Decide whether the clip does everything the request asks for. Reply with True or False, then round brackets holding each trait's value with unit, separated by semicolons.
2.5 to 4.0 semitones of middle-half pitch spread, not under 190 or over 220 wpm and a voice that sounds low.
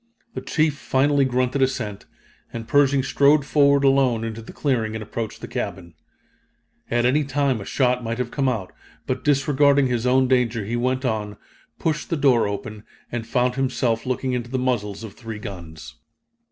False (3.4 semitones; 175 wpm; 125 Hz)